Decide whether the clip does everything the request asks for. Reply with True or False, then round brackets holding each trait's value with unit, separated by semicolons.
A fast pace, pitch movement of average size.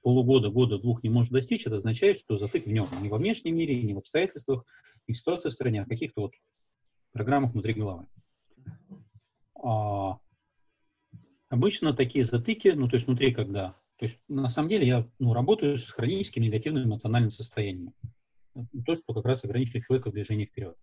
True (180 wpm; 3.5 semitones)